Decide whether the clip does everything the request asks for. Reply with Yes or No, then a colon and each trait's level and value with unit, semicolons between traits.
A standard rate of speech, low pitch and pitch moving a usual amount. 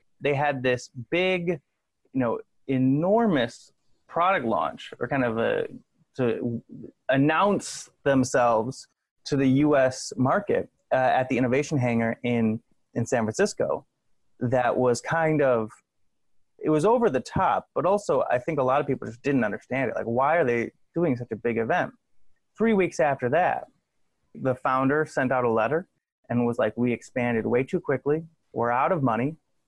Yes: average, 165 wpm; low, 130 Hz; average, 4.5 semitones